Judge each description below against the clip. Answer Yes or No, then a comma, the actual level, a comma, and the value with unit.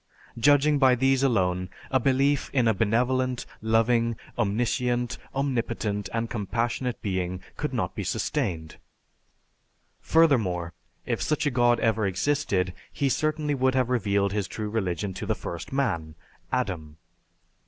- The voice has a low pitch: Yes, low, 115 Hz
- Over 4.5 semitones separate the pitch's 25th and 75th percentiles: Yes, average, 4.9 semitones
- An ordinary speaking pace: No, slow, 130 wpm